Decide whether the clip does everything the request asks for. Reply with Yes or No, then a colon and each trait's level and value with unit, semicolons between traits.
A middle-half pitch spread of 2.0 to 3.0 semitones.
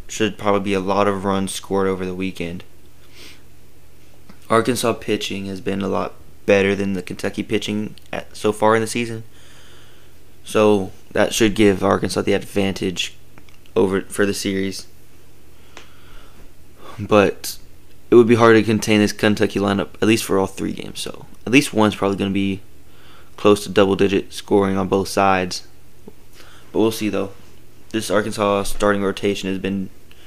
Yes: average, 2.7 semitones